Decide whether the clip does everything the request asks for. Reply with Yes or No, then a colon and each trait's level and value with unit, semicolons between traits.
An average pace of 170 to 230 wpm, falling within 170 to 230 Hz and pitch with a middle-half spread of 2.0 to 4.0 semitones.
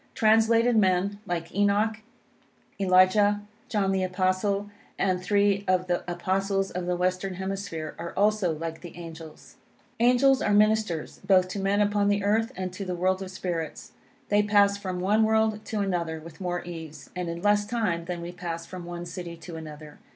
Yes: average, 175 wpm; medium, 185 Hz; average, 2.8 semitones